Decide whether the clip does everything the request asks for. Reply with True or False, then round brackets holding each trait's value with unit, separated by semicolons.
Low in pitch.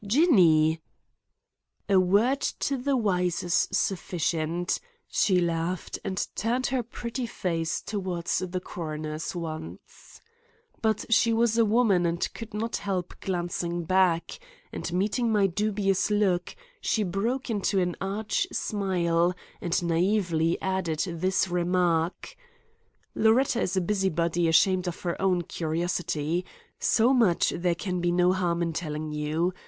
False (180 Hz)